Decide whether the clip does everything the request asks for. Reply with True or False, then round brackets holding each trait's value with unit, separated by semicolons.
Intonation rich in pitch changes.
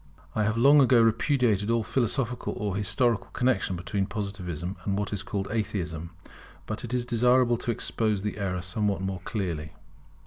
False (3.6 semitones)